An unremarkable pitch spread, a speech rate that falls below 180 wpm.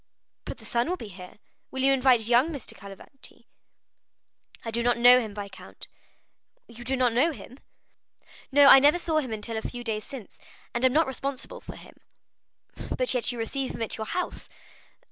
No: average, 3.1 semitones; average, 185 wpm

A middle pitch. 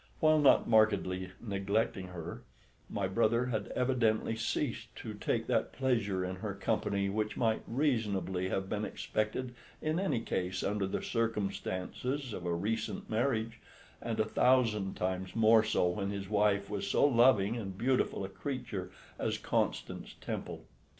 No: low, 105 Hz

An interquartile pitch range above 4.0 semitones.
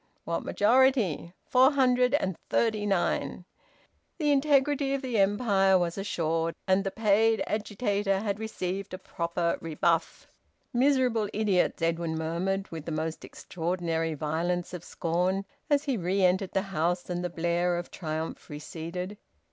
Yes: average, 4.5 semitones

